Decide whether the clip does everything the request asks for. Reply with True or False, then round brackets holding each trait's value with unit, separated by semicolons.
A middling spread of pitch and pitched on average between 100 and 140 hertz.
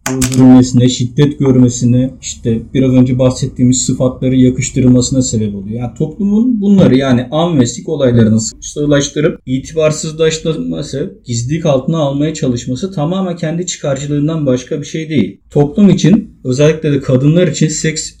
True (3.8 semitones; 135 Hz)